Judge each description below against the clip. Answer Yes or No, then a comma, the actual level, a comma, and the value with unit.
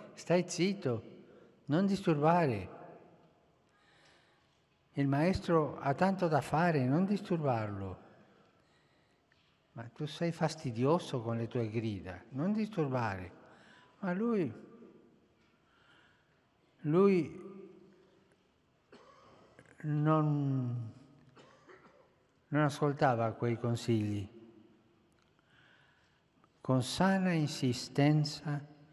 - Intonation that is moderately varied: No, wide, 6.3 semitones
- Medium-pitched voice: Yes, medium, 145 Hz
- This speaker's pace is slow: Yes, slow, 70 wpm